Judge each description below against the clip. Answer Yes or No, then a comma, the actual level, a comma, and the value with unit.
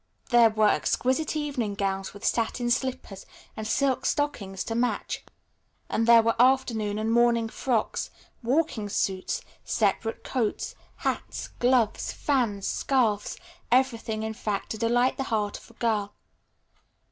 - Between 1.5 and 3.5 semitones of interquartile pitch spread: Yes, average, 3.1 semitones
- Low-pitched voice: No, high, 230 Hz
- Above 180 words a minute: No, slow, 135 wpm